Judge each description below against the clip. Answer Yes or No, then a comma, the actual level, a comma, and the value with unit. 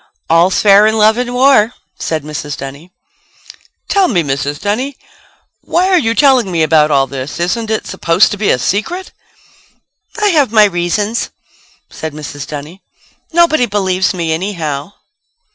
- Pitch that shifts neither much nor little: No, wide, 6.9 semitones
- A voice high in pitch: Yes, high, 195 Hz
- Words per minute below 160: Yes, average, 150 wpm